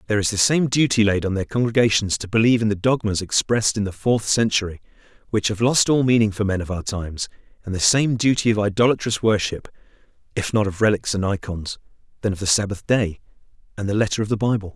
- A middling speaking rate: No, fast, 215 wpm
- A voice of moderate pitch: No, low, 105 Hz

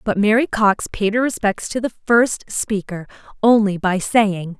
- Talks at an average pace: Yes, average, 170 wpm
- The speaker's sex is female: Yes, female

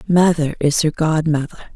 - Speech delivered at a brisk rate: No, slow, 135 wpm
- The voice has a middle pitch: Yes, medium, 155 Hz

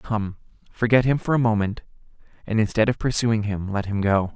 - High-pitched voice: No, low, 110 Hz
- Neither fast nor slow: Yes, average, 195 wpm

